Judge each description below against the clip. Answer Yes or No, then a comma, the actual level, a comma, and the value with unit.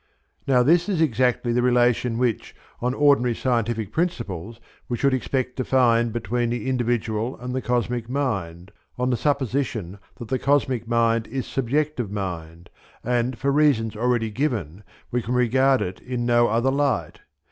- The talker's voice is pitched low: Yes, low, 120 Hz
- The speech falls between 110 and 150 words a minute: No, average, 160 wpm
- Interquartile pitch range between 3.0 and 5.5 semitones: No, narrow, 2.4 semitones